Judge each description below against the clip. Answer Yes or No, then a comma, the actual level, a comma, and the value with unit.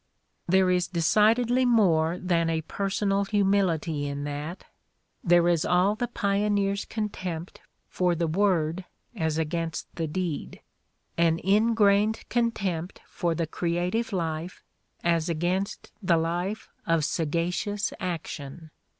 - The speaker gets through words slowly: Yes, slow, 125 wpm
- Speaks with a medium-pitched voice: Yes, medium, 180 Hz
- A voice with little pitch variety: No, average, 3.4 semitones